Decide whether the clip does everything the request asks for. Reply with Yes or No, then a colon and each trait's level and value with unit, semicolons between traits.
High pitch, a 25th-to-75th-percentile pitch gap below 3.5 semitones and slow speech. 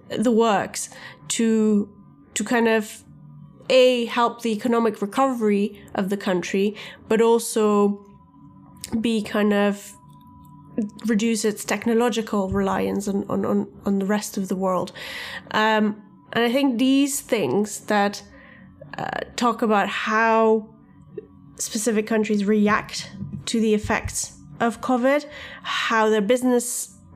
Yes: high, 220 Hz; narrow, 2.4 semitones; slow, 120 wpm